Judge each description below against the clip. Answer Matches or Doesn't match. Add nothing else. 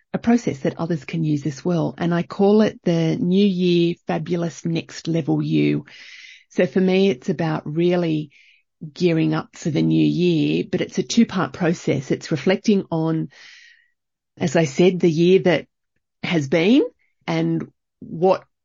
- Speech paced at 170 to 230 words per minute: Doesn't match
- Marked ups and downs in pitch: Doesn't match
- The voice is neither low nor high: Matches